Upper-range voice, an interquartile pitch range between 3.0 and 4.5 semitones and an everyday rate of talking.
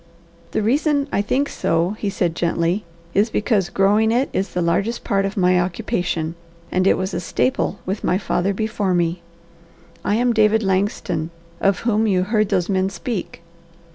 Yes: high, 195 Hz; average, 3.3 semitones; average, 170 wpm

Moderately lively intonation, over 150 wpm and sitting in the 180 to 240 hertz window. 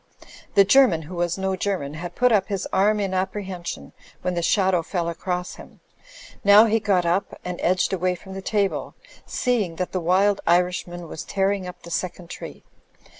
No: narrow, 2.3 semitones; average, 180 wpm; medium, 185 Hz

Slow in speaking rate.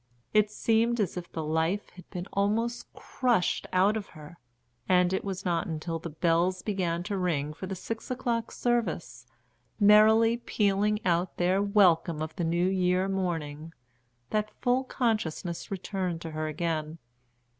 No: average, 155 wpm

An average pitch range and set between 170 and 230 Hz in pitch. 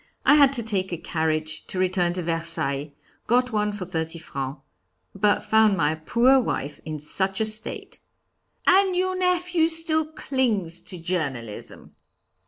No: wide, 8.2 semitones; high, 190 Hz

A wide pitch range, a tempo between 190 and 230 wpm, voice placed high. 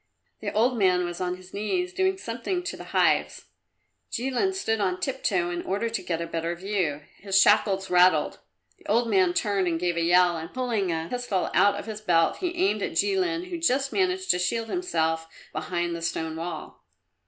Yes: wide, 6.5 semitones; average, 195 wpm; high, 195 Hz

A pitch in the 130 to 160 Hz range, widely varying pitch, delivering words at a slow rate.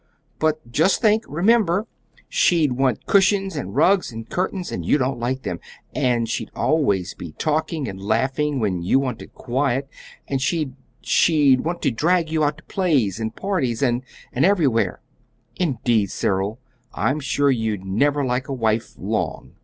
No: low, 135 Hz; wide, 5.8 semitones; average, 160 wpm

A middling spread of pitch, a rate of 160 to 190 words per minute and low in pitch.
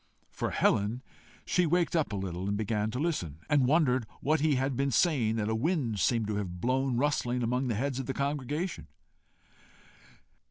Yes: average, 5.0 semitones; average, 175 wpm; low, 125 Hz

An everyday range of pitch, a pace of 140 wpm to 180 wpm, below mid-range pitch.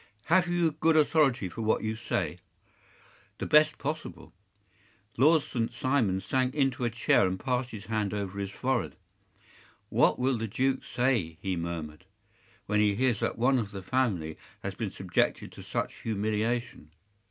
Yes: average, 5.0 semitones; average, 160 wpm; low, 115 Hz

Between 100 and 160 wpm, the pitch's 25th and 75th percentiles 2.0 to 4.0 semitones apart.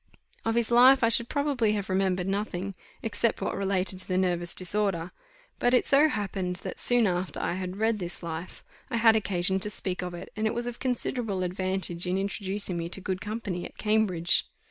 No: average, 200 wpm; average, 3.6 semitones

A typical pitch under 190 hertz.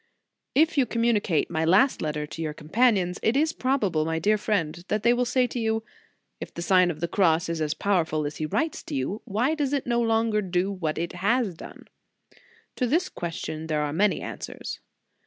No: high, 195 Hz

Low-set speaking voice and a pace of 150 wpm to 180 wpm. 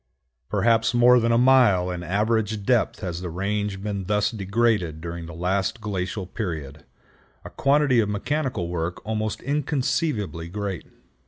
No: low, 105 Hz; average, 140 wpm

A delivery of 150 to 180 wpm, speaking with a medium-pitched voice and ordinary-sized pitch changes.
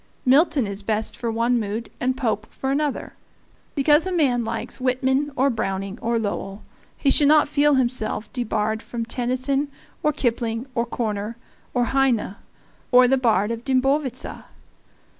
No: average, 155 wpm; high, 245 Hz; average, 3.3 semitones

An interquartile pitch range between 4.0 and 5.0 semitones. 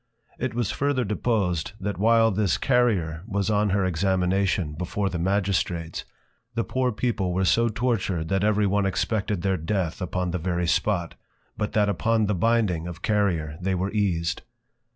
No: average, 3.3 semitones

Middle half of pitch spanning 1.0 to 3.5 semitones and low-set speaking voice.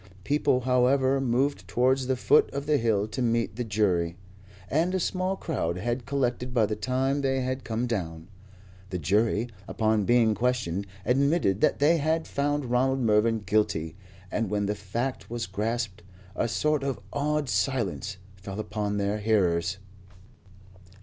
No: average, 4.5 semitones; low, 120 Hz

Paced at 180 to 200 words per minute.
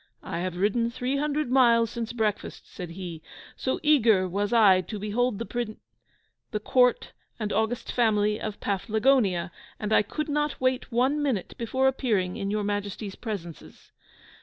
No: average, 160 wpm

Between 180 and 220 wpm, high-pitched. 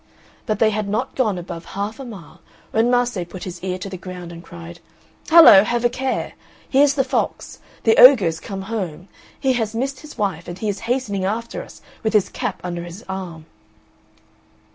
Yes: average, 195 wpm; high, 210 Hz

